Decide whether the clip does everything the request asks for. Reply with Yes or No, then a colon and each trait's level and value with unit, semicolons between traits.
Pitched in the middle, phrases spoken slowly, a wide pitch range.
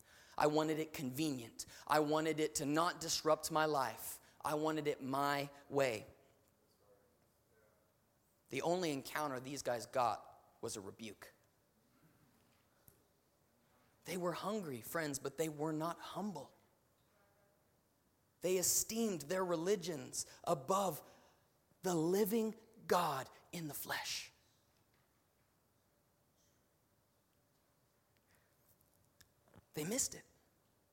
Yes: medium, 150 Hz; slow, 95 wpm; wide, 5.8 semitones